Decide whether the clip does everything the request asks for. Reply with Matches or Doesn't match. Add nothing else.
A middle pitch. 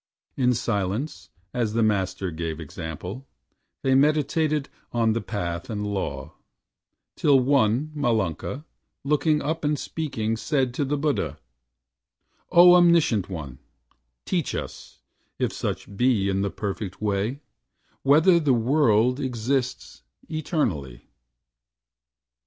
Doesn't match